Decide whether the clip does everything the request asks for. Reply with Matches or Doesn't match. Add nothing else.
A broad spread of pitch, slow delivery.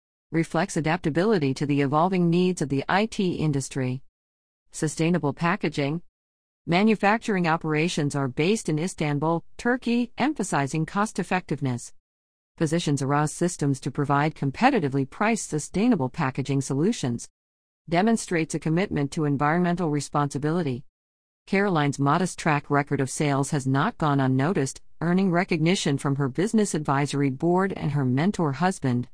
Doesn't match